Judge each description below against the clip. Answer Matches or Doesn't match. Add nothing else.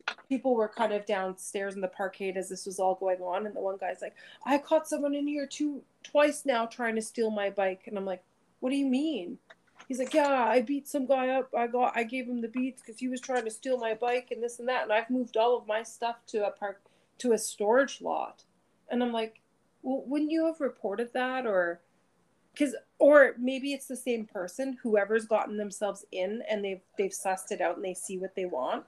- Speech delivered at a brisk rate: Matches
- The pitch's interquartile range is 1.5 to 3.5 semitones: Doesn't match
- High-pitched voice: Matches